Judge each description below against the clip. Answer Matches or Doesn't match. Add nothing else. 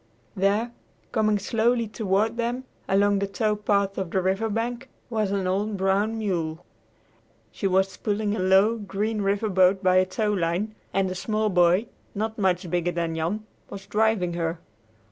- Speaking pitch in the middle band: Doesn't match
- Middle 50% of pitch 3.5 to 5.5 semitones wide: Doesn't match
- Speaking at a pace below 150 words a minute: Doesn't match